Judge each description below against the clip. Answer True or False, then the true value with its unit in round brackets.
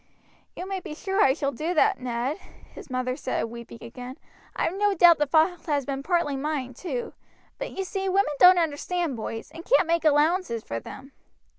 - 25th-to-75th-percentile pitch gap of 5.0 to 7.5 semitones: True (5.6 semitones)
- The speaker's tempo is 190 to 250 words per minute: True (195 wpm)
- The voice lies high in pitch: True (310 Hz)